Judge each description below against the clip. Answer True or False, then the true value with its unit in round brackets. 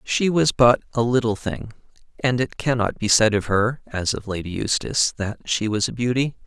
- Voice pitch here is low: True (120 Hz)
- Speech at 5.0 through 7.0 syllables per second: True (5.1 syllables/s)